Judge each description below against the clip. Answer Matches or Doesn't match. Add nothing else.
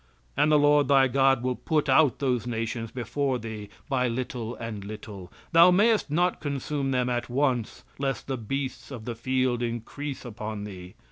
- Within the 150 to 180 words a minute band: Matches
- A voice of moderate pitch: Doesn't match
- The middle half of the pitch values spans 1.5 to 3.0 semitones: Doesn't match